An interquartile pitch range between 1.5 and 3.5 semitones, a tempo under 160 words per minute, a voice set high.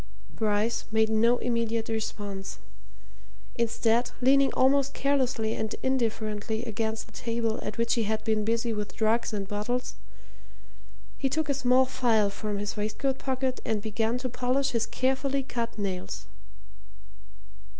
Yes: average, 2.8 semitones; average, 140 wpm; high, 230 Hz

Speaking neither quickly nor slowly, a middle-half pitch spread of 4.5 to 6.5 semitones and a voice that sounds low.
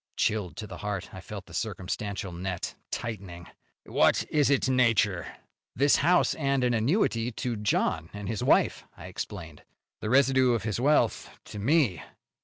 Yes: average, 160 wpm; average, 5.0 semitones; low, 110 Hz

